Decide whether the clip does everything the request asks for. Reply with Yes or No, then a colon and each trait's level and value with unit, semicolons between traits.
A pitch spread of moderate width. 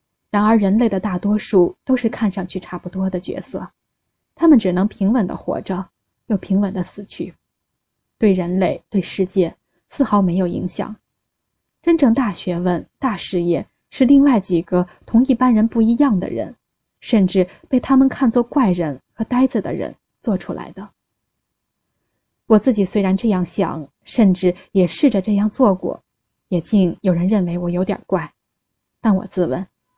Yes: average, 3.8 semitones